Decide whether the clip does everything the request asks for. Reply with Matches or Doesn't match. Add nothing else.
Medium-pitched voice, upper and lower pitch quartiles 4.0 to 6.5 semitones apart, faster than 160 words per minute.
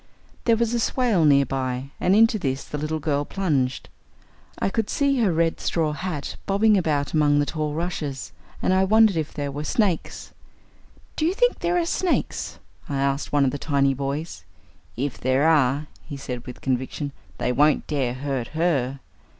Matches